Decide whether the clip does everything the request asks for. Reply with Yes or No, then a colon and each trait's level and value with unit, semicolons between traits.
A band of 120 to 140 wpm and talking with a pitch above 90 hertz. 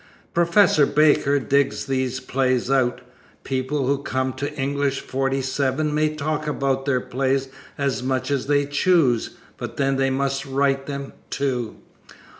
Yes: slow, 135 wpm; low, 135 Hz